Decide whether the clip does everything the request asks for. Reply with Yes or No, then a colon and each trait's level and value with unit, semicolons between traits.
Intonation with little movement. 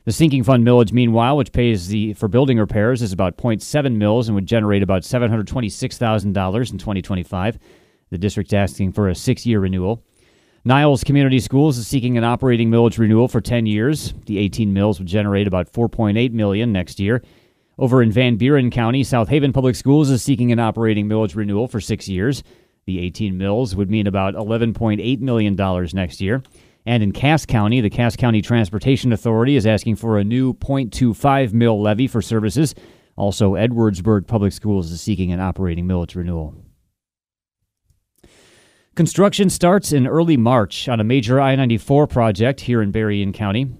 No: average, 3.8 semitones